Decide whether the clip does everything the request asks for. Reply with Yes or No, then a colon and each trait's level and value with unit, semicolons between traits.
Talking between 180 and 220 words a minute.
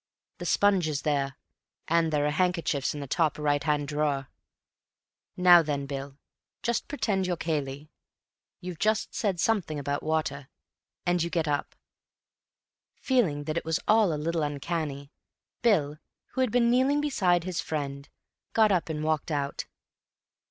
No: average, 150 wpm